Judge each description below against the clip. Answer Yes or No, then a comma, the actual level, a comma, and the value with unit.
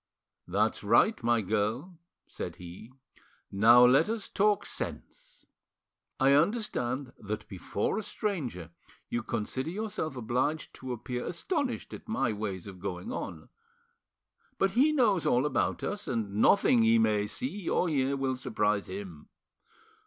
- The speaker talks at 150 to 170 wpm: No, average, 140 wpm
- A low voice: Yes, low, 130 Hz